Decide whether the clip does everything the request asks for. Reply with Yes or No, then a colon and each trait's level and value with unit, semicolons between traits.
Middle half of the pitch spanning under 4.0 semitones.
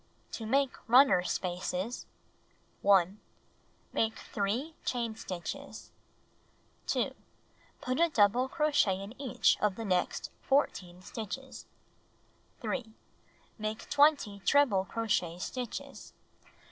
No: average, 5.3 semitones